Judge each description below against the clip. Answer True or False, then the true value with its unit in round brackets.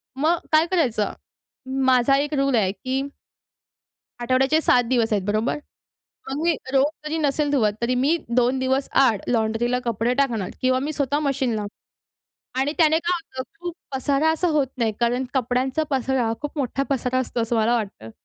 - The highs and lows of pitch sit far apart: False (3.3 semitones)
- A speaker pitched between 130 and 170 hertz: False (260 Hz)